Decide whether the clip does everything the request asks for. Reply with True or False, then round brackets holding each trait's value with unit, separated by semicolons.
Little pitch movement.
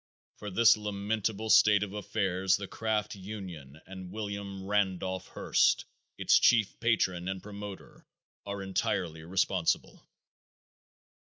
True (2.0 semitones)